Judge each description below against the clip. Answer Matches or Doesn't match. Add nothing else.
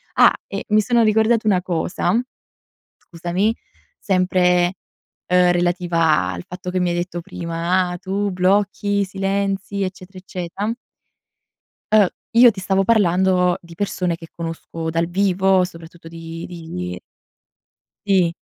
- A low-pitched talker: Doesn't match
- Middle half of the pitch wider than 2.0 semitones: Matches